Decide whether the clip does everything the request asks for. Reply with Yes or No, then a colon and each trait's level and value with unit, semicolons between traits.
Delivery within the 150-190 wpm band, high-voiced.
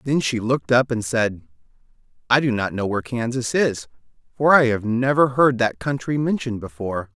No: average, 185 wpm; low, 120 Hz